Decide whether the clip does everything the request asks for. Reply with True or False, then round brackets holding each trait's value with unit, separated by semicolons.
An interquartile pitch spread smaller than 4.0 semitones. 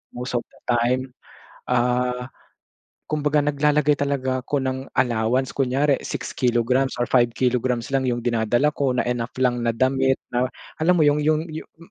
True (2.6 semitones)